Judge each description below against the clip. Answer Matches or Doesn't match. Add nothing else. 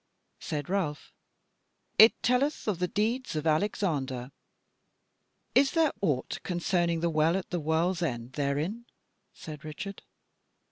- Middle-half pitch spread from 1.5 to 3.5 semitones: Doesn't match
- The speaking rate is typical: Doesn't match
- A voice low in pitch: Doesn't match